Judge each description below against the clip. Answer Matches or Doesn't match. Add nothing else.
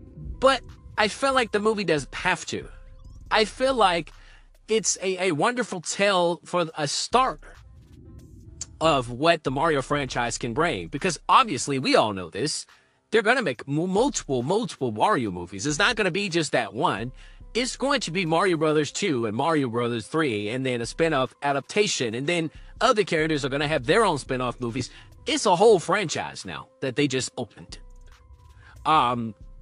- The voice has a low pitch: Doesn't match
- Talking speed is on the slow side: Doesn't match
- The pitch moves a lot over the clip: Matches